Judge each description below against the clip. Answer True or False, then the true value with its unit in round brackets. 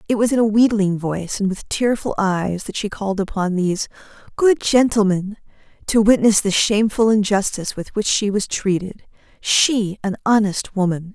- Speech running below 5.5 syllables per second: True (5.1 syllables/s)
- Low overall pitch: False (205 Hz)